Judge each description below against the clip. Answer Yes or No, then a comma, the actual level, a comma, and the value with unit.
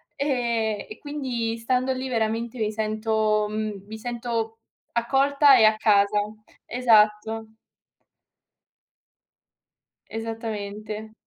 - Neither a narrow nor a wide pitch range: No, narrow, 2.1 semitones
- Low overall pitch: No, high, 225 Hz